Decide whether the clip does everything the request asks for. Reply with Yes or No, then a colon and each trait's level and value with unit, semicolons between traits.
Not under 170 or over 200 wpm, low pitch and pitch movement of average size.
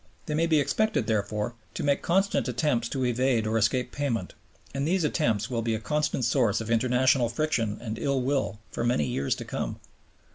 Yes: average, 190 wpm; low, 125 Hz; average, 4.1 semitones